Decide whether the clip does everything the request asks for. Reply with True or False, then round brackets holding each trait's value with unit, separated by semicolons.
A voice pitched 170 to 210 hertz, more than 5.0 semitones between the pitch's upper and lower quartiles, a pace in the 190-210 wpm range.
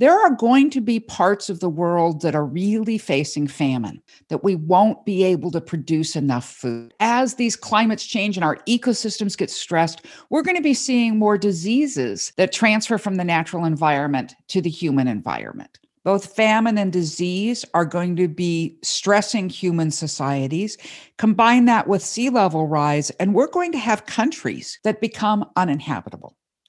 False (190 Hz; 5.4 semitones; 170 wpm)